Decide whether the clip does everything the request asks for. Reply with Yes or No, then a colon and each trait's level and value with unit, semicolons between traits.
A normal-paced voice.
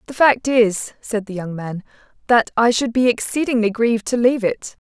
Yes: average, 195 wpm